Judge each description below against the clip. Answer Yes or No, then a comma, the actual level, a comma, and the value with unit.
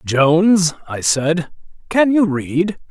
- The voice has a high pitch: No, medium, 170 Hz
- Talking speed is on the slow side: Yes, slow, 125 wpm